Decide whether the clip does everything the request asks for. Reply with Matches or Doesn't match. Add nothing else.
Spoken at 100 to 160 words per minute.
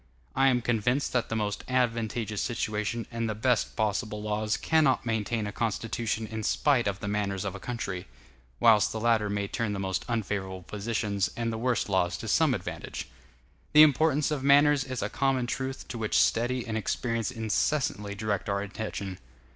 Doesn't match